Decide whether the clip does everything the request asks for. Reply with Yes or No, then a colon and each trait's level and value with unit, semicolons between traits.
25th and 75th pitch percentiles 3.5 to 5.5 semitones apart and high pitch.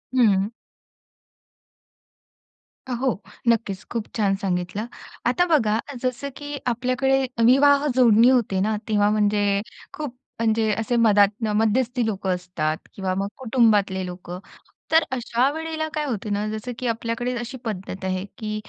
Yes: average, 3.9 semitones; high, 225 Hz